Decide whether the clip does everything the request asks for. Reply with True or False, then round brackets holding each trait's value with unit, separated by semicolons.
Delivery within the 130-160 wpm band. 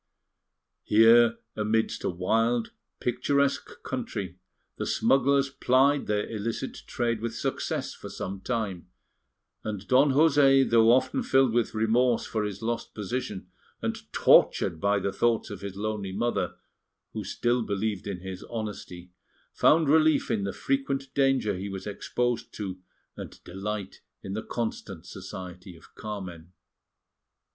True (135 wpm)